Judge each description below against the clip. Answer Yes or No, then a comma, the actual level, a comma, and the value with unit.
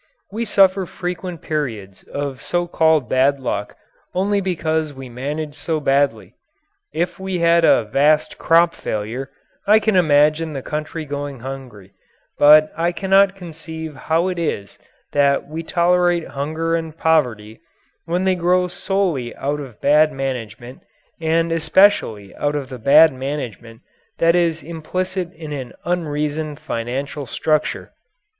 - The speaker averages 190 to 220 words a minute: No, slow, 135 wpm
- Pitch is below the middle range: No, medium, 155 Hz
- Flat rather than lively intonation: No, average, 4.0 semitones